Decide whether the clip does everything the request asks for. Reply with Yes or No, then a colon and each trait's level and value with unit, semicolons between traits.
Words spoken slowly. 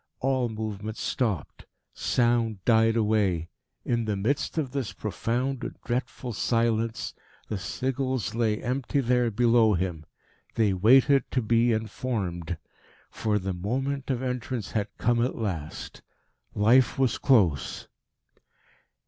Yes: slow, 125 wpm